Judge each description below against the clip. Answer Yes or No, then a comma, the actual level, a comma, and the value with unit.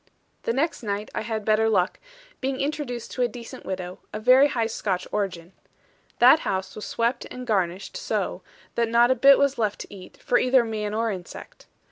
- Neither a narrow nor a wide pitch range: Yes, average, 3.8 semitones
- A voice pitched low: No, high, 225 Hz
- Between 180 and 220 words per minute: Yes, average, 190 wpm